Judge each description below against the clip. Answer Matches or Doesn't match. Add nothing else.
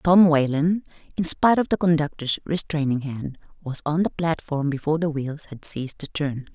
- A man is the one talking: Doesn't match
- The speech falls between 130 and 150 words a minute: Doesn't match